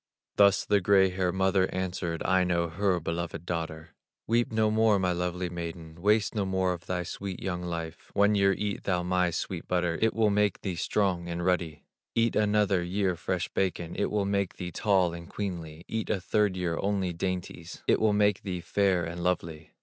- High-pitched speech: No, very low, 90 Hz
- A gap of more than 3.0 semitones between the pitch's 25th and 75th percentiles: No, average, 2.7 semitones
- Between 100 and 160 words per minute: No, average, 195 wpm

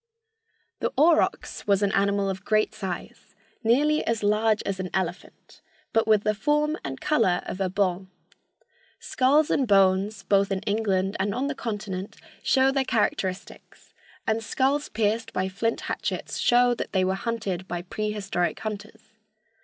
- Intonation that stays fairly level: No, average, 3.2 semitones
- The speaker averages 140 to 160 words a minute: Yes, average, 155 wpm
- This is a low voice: No, high, 205 Hz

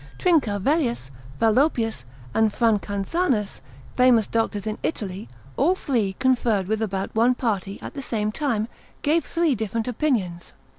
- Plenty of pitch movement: No, average, 4.2 semitones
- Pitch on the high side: Yes, high, 225 Hz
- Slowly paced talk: Yes, slow, 130 wpm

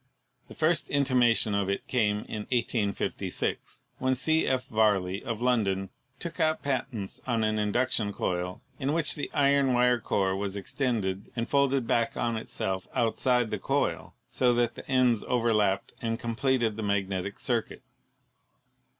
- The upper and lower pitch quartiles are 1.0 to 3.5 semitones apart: No, average, 4.0 semitones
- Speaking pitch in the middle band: No, low, 115 Hz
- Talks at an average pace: Yes, average, 155 wpm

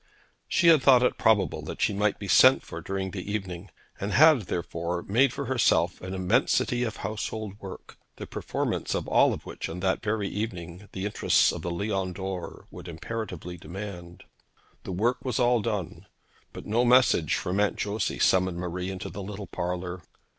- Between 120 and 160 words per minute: No, average, 175 wpm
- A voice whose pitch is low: Yes, low, 100 Hz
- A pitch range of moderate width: Yes, average, 3.6 semitones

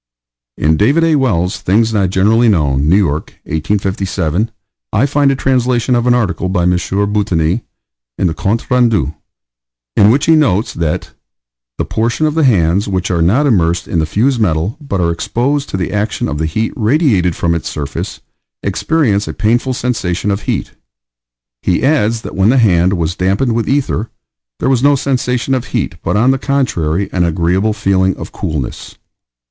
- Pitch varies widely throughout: Yes, wide, 6.0 semitones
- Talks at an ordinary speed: Yes, average, 175 wpm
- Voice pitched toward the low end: Yes, low, 105 Hz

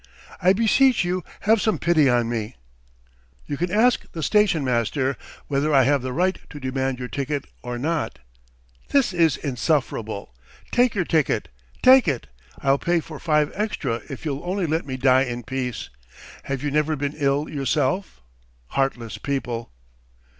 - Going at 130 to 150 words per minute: No, average, 160 wpm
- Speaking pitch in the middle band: Yes, medium, 145 Hz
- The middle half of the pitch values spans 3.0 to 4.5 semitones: No, average, 5.0 semitones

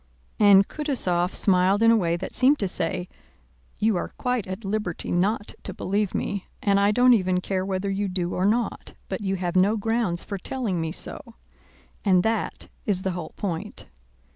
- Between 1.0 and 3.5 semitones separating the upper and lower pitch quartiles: Yes, average, 2.9 semitones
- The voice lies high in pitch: Yes, high, 195 Hz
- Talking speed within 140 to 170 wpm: No, average, 185 wpm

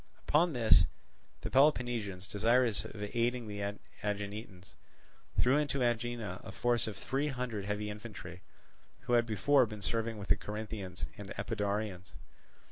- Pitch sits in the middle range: No, low, 110 Hz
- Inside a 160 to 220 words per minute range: No, slow, 135 wpm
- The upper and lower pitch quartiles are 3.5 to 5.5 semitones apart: No, average, 3.1 semitones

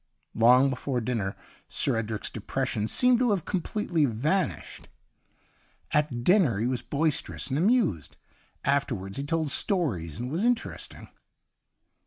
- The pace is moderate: No, slow, 130 wpm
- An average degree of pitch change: No, wide, 7.0 semitones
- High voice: No, medium, 140 Hz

